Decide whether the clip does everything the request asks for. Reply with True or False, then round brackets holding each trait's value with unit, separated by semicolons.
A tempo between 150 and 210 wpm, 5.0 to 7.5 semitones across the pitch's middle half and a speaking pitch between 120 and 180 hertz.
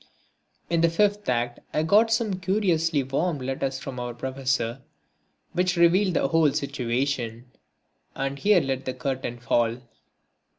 False (135 wpm; 5.4 semitones; 135 Hz)